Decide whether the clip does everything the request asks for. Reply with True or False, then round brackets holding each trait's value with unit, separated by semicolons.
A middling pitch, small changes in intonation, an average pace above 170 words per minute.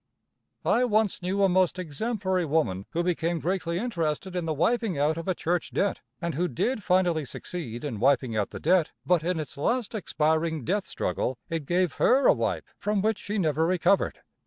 False (175 Hz; 3.6 semitones; 190 wpm)